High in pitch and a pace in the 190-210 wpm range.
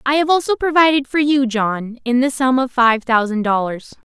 Yes: very high, 255 Hz; fast, 205 wpm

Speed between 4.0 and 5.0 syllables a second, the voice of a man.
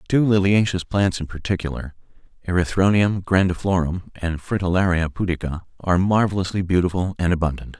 No: 5.8 syllables/s; male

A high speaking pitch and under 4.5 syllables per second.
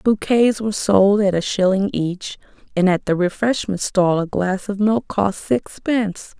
Yes: high, 200 Hz; 4.3 syllables/s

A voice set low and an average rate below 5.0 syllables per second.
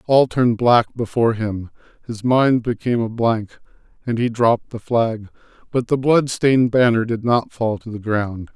Yes: low, 115 Hz; 4.7 syllables/s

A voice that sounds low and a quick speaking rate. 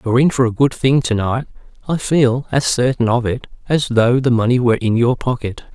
Yes: low, 125 Hz; fast, 230 wpm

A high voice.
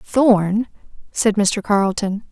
Yes: high, 210 Hz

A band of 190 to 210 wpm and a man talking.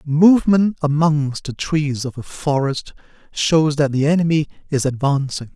No: average, 140 wpm; male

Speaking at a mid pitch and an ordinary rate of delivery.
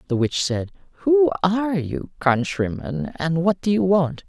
Yes: medium, 155 Hz; average, 170 wpm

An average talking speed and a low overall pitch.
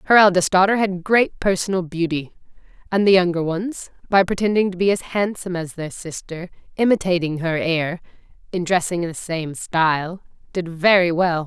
No: average, 165 wpm; medium, 180 Hz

